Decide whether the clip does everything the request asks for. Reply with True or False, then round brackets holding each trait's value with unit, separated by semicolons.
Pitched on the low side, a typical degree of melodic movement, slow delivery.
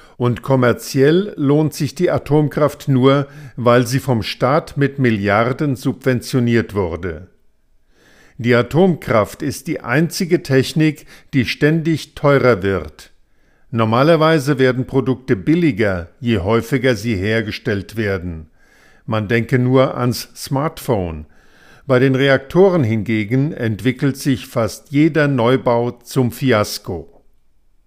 True (130 Hz; 4.0 semitones; 110 wpm)